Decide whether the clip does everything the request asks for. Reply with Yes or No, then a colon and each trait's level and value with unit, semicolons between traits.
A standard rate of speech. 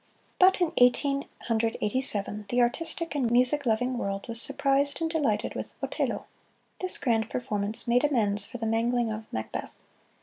Yes: average, 165 wpm